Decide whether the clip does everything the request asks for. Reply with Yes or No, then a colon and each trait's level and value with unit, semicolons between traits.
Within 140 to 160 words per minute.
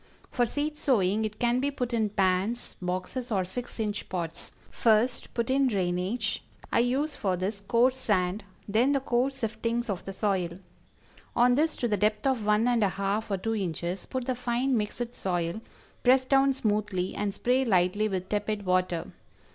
No: average, 180 wpm